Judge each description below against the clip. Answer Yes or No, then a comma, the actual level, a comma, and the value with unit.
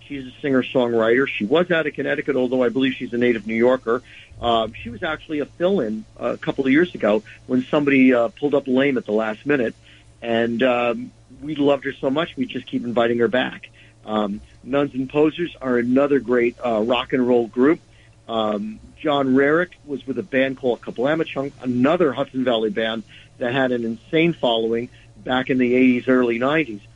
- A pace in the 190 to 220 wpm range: Yes, average, 195 wpm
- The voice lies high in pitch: No, low, 125 Hz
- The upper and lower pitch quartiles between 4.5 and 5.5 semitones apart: No, average, 3.2 semitones